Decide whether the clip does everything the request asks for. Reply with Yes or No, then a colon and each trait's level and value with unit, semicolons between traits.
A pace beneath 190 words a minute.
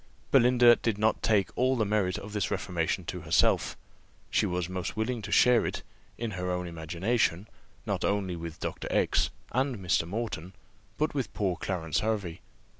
Yes: average, 170 wpm